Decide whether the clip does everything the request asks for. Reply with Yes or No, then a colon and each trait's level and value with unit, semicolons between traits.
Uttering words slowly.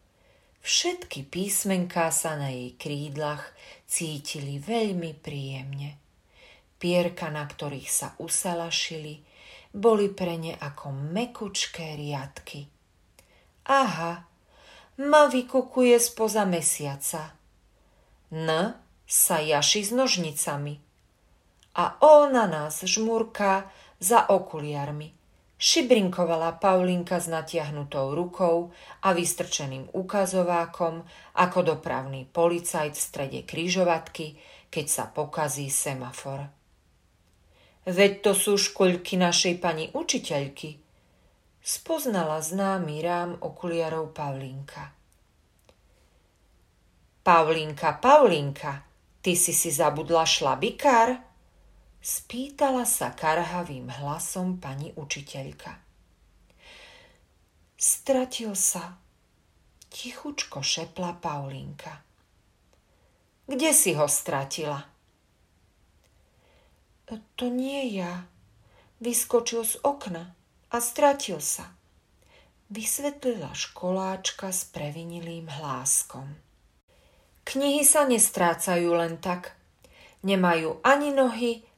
Yes: slow, 80 wpm